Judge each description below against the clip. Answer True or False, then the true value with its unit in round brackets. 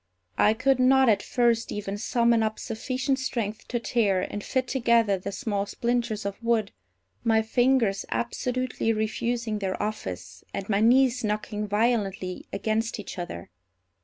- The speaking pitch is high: True (225 Hz)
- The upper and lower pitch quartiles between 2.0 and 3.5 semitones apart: True (2.9 semitones)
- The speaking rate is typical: True (145 wpm)